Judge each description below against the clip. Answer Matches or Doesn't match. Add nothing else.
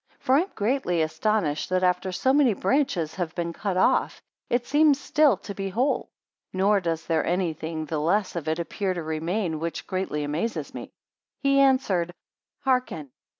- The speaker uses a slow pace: Doesn't match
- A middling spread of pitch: Doesn't match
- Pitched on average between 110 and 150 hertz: Doesn't match